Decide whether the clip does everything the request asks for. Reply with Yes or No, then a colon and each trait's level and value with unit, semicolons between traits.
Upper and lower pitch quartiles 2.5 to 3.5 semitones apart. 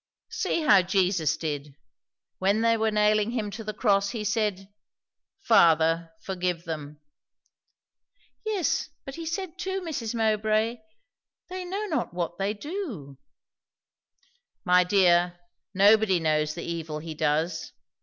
No: average, 5.2 semitones